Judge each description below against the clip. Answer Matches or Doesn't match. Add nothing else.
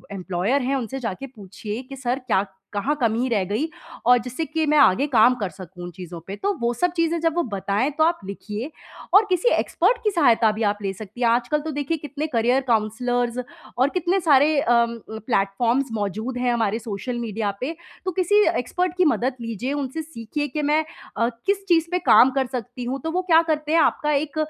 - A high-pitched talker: Matches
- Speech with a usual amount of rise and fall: Doesn't match